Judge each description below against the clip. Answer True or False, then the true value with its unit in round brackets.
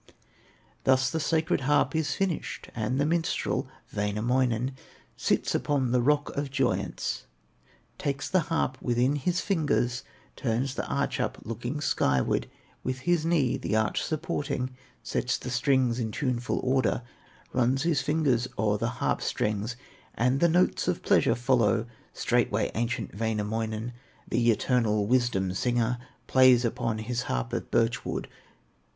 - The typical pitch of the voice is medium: False (125 Hz)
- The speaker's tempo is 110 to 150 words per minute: True (140 wpm)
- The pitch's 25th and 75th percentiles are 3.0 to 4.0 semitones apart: True (3.3 semitones)